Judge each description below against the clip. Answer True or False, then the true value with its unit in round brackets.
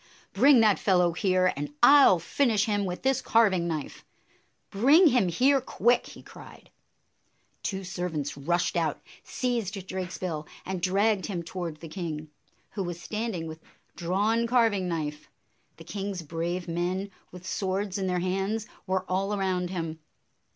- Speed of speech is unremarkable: True (150 wpm)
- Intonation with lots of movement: False (3.3 semitones)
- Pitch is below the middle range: False (185 Hz)